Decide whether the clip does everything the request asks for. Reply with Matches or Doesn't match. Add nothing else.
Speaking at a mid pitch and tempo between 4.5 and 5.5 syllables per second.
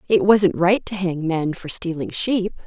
Doesn't match